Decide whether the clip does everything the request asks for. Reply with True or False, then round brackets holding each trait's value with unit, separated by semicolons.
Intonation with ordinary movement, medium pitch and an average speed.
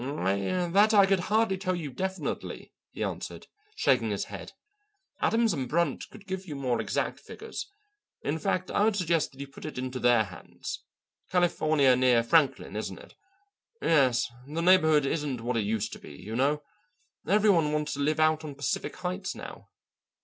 False (6.1 semitones; 155 Hz; 175 wpm)